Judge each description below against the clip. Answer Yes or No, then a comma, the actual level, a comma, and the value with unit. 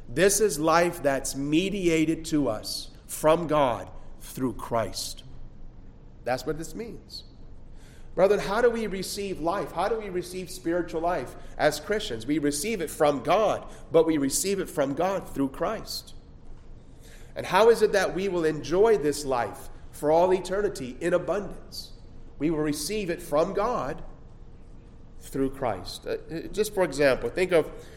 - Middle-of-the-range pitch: Yes, medium, 170 Hz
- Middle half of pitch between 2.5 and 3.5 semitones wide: No, average, 4.6 semitones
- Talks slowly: No, average, 150 wpm